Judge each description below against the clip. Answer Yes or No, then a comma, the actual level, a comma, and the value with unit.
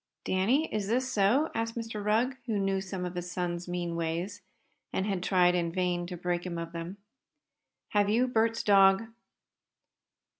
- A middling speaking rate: Yes, average, 165 wpm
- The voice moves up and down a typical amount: Yes, average, 3.9 semitones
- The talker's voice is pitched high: Yes, high, 195 Hz